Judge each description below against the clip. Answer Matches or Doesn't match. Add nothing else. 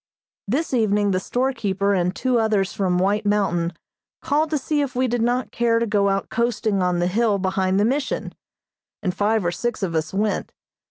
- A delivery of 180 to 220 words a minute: Matches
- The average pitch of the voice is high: Matches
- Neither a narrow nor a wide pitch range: Matches